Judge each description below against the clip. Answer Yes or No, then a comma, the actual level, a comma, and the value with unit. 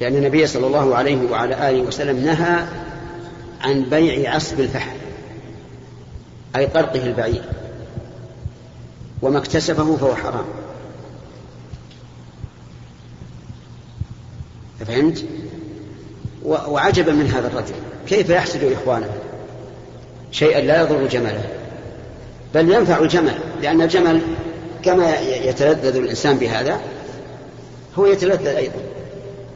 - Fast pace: No, average, 90 wpm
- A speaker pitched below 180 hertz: Yes, medium, 140 Hz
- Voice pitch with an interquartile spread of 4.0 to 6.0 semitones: Yes, average, 4.4 semitones